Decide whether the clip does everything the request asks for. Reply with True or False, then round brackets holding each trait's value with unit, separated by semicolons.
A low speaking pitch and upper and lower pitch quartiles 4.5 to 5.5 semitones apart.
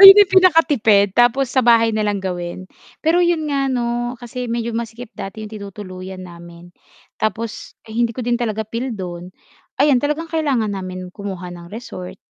False (225 Hz; 4.9 semitones)